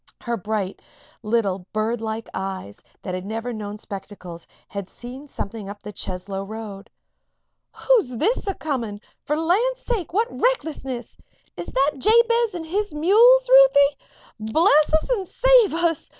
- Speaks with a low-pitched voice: No, very high, 255 Hz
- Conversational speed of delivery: Yes, average, 150 wpm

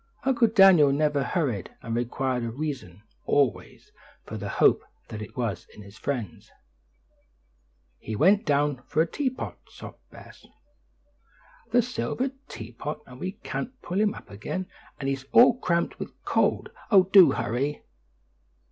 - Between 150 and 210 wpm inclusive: No, average, 140 wpm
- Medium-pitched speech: Yes, medium, 145 Hz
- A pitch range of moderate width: No, wide, 8.1 semitones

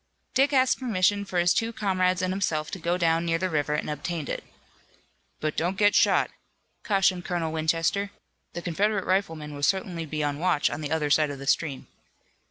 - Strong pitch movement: No, average, 3.8 semitones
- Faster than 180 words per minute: Yes, average, 190 wpm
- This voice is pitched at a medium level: Yes, medium, 175 Hz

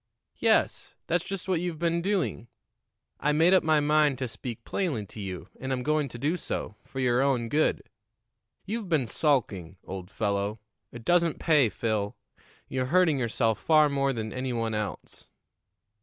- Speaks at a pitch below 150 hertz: Yes, low, 135 Hz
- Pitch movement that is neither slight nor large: No, wide, 6.0 semitones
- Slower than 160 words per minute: No, average, 170 wpm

